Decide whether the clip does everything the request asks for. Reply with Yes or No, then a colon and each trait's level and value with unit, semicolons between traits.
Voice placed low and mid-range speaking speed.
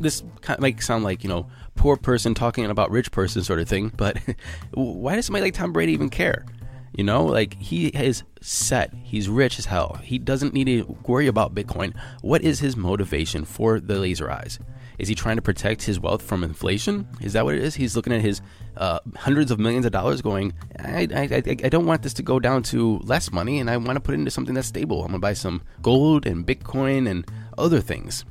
No: low, 115 Hz; fast, 230 wpm